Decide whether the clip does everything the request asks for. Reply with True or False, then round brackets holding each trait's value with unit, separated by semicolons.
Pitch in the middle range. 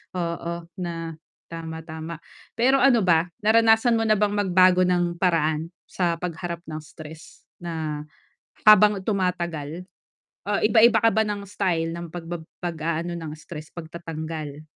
True (170 Hz)